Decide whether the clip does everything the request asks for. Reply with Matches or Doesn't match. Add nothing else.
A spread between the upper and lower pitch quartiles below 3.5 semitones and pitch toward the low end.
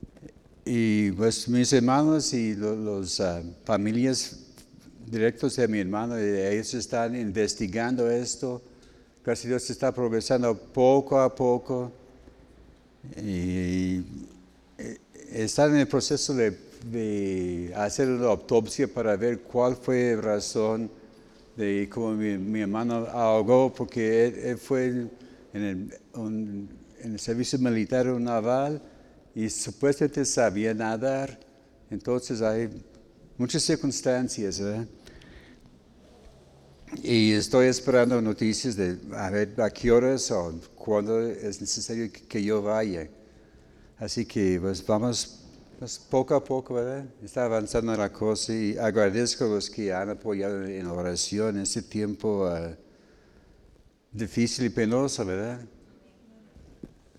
Matches